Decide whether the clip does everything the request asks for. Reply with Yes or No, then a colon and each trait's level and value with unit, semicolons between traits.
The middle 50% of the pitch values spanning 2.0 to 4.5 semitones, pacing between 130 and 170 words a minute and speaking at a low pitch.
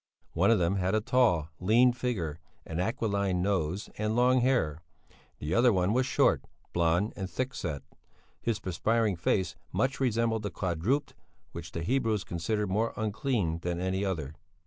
No: average, 5.1 semitones; average, 160 wpm; low, 100 Hz